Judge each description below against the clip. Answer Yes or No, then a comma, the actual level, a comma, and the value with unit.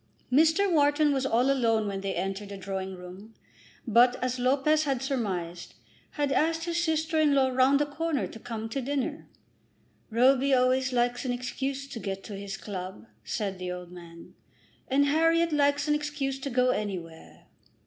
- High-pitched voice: Yes, very high, 255 Hz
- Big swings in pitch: Yes, wide, 6.2 semitones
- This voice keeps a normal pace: Yes, average, 170 wpm